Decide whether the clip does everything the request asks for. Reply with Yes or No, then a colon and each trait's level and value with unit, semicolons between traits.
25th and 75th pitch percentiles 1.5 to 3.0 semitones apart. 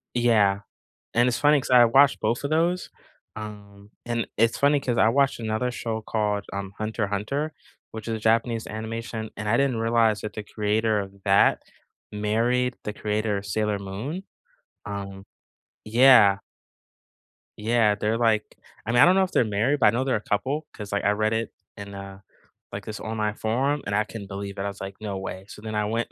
Yes: narrow, 2.6 semitones